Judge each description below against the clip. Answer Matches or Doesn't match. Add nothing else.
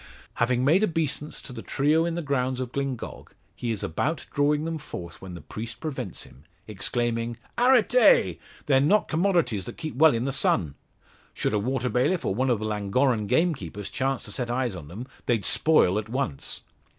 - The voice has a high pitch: Doesn't match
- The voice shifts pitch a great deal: Matches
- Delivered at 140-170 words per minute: Doesn't match